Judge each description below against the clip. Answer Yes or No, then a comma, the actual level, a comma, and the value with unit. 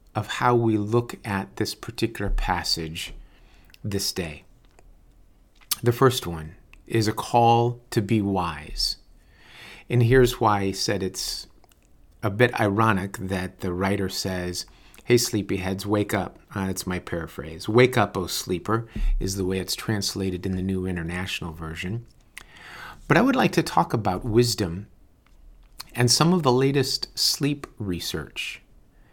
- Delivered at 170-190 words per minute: No, average, 145 wpm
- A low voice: Yes, low, 100 Hz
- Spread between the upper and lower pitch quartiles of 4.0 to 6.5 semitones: Yes, average, 4.5 semitones